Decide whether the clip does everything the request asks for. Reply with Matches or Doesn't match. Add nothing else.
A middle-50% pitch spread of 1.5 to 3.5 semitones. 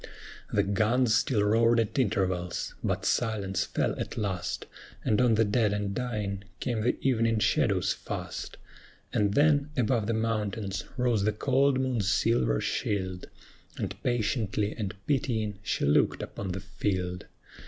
Matches